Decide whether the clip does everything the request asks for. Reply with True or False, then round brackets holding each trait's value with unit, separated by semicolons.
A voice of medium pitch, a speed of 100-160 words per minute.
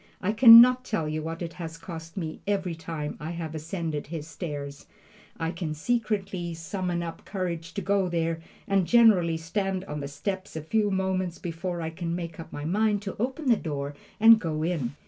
False (170 Hz; 195 wpm)